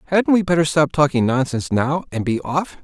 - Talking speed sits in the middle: No, fast, 210 wpm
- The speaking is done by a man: Yes, male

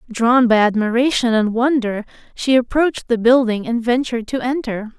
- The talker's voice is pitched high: Yes, high, 240 Hz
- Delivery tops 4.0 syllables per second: Yes, 5.4 syllables/s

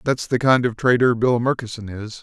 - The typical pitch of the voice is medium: No, low, 120 Hz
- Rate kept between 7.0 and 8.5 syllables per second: No, 5.2 syllables/s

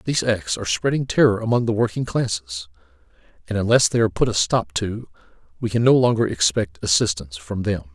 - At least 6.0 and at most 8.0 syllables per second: Yes, 6.1 syllables/s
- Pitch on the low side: Yes, low, 100 Hz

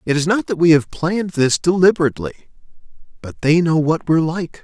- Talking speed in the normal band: Yes, average, 195 wpm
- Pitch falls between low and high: Yes, medium, 160 Hz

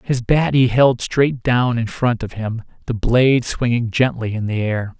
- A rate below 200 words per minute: No, fast, 205 wpm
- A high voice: No, low, 120 Hz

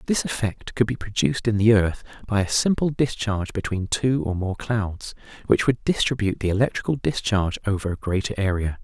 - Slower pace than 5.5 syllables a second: No, 5.6 syllables/s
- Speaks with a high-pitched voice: No, low, 105 Hz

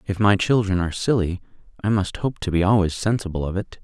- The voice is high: No, very low, 95 Hz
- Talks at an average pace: No, fast, 220 wpm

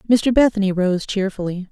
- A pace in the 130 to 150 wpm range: Yes, average, 140 wpm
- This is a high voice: Yes, high, 200 Hz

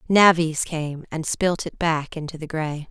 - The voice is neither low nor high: Yes, medium, 160 Hz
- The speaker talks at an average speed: Yes, average, 185 wpm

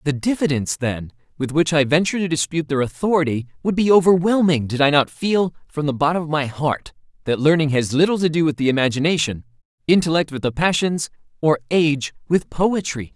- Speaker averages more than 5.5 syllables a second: Yes, 5.9 syllables/s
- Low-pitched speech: No, medium, 155 Hz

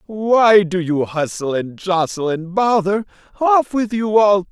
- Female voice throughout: No, male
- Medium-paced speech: Yes, average, 160 wpm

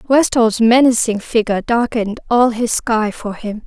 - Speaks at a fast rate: No, average, 145 wpm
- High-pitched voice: Yes, high, 230 Hz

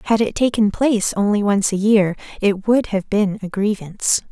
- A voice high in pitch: Yes, high, 205 Hz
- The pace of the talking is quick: No, average, 195 wpm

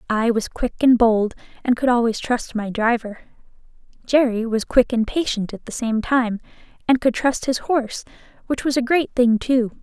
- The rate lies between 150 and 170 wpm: No, average, 190 wpm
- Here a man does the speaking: No, female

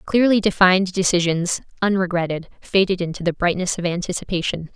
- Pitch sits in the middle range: Yes, medium, 180 Hz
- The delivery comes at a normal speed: No, slow, 125 wpm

